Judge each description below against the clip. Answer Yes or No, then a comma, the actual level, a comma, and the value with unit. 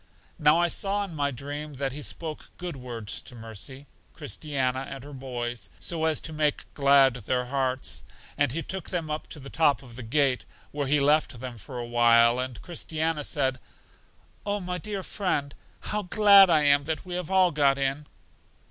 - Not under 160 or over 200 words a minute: Yes, average, 190 wpm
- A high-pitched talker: No, medium, 145 Hz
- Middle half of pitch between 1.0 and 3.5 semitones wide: No, average, 3.9 semitones